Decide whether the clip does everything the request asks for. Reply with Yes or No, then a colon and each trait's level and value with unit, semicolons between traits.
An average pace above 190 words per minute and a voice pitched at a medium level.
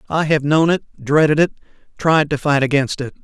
No: average, 165 wpm; medium, 150 Hz